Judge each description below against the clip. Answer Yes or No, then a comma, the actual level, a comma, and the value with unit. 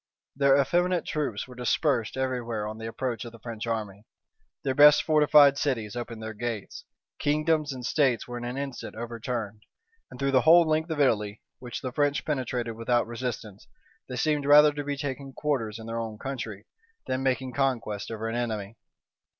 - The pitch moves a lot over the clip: No, average, 3.9 semitones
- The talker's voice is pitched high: No, low, 125 Hz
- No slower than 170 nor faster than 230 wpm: Yes, average, 185 wpm